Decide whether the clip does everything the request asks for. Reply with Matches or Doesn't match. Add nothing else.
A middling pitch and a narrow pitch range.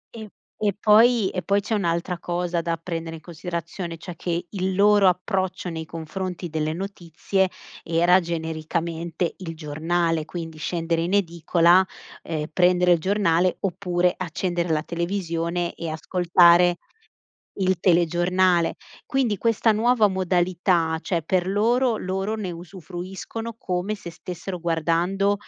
Matches